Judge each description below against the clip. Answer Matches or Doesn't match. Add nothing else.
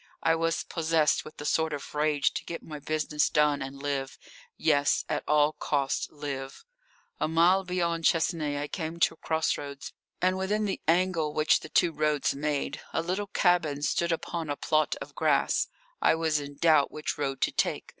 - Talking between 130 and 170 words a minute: Doesn't match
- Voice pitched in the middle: Matches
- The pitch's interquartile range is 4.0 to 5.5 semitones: Doesn't match